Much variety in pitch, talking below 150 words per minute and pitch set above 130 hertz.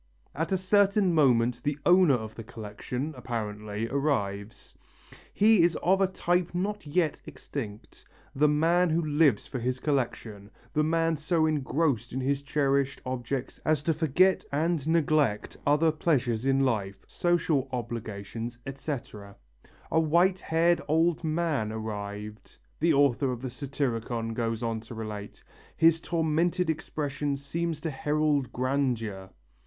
Yes: wide, 5.7 semitones; average, 140 wpm; medium, 140 Hz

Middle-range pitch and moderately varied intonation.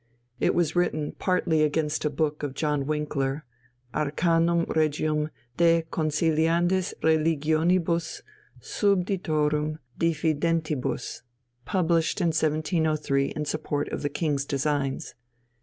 No: medium, 155 Hz; narrow, 1.9 semitones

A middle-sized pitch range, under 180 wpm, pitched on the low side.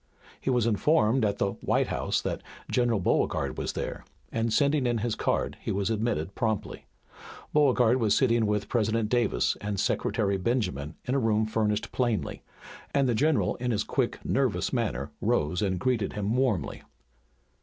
Yes: average, 3.1 semitones; average, 165 wpm; low, 110 Hz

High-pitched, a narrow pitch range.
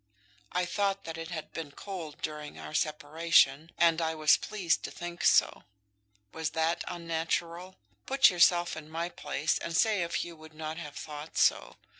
No: medium, 165 Hz; narrow, 1.9 semitones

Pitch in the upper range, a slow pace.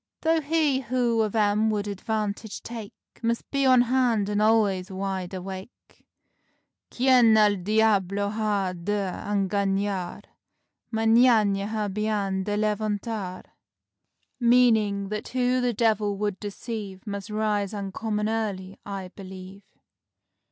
Yes: high, 210 Hz; slow, 115 wpm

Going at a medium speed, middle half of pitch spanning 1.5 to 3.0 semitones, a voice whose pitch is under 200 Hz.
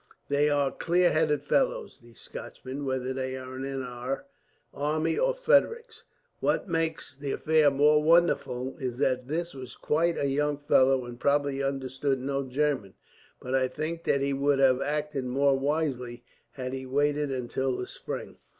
Yes: average, 160 wpm; narrow, 2.4 semitones; medium, 140 Hz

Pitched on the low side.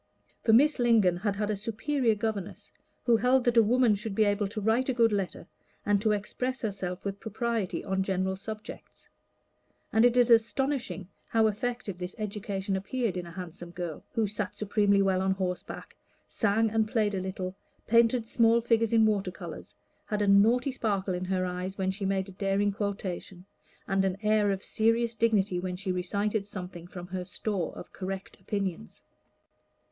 No: high, 205 Hz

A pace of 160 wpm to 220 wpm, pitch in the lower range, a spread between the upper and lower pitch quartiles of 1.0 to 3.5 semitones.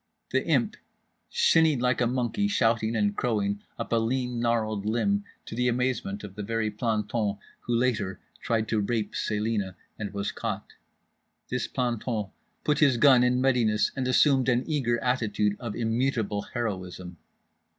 No: average, 150 wpm; low, 115 Hz; average, 3.0 semitones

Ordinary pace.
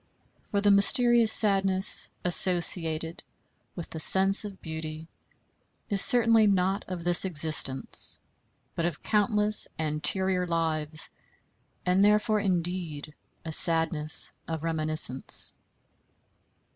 No: slow, 100 wpm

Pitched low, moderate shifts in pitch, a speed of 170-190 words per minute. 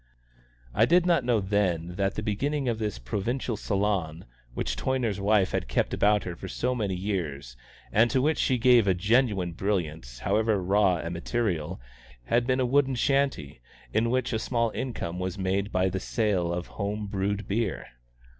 Yes: low, 100 Hz; average, 4.5 semitones; average, 175 wpm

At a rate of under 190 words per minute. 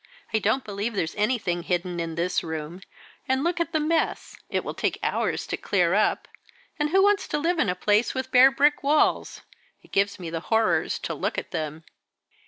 No: fast, 205 wpm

